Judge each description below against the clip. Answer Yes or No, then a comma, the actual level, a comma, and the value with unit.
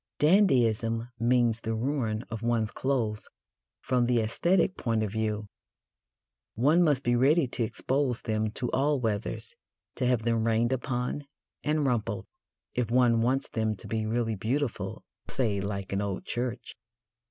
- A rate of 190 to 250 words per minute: No, average, 150 wpm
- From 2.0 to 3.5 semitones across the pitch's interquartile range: Yes, average, 2.9 semitones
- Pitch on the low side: Yes, low, 120 Hz